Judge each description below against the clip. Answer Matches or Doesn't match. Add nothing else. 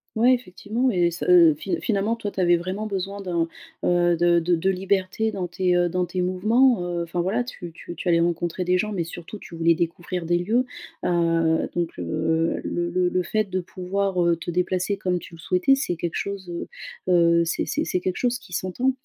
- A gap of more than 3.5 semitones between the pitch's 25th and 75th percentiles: Doesn't match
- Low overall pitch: Doesn't match